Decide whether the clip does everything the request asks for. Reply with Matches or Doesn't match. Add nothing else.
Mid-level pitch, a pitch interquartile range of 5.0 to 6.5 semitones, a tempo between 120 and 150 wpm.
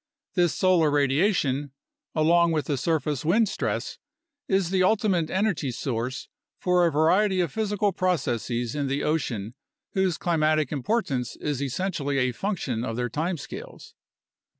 Matches